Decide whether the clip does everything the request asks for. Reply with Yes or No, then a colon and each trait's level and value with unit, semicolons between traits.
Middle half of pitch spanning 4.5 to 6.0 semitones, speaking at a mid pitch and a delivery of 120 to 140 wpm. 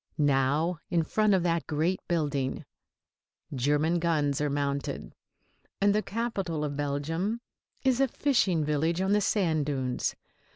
Yes: average, 4.8 semitones; medium, 160 Hz; slow, 135 wpm